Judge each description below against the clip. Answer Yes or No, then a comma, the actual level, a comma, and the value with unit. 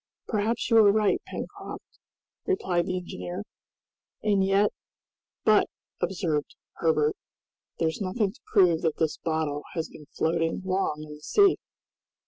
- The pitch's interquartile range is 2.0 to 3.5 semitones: No, average, 4.3 semitones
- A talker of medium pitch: Yes, medium, 180 Hz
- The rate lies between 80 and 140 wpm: Yes, slow, 135 wpm